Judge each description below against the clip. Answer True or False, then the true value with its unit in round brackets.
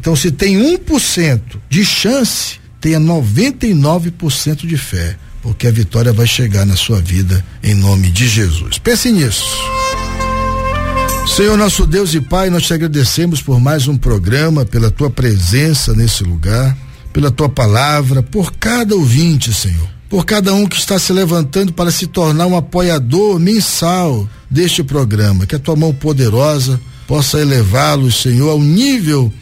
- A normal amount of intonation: False (7.5 semitones)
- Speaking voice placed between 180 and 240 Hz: False (140 Hz)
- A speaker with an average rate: True (155 wpm)